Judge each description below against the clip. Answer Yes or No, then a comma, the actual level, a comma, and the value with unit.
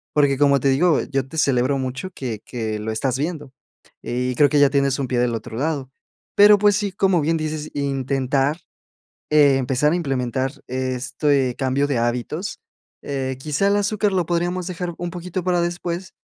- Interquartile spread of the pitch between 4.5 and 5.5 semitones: Yes, average, 4.9 semitones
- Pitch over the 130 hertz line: Yes, medium, 140 Hz